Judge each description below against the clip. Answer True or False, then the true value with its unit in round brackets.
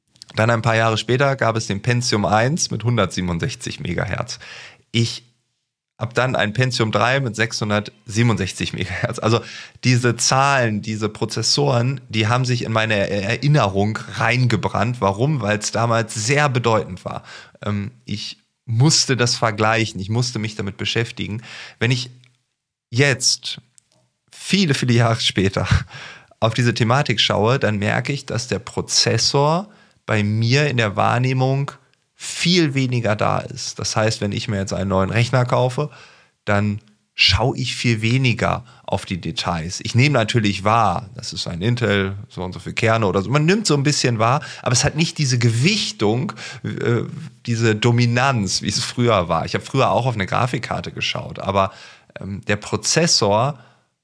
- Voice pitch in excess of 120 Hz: False (115 Hz)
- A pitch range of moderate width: True (3.5 semitones)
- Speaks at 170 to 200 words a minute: False (155 wpm)